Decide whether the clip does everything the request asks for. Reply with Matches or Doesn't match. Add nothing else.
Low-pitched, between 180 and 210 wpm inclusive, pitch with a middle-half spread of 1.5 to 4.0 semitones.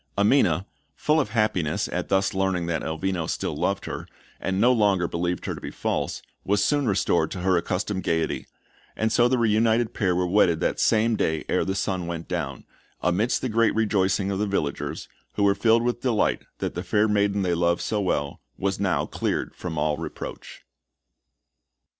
Matches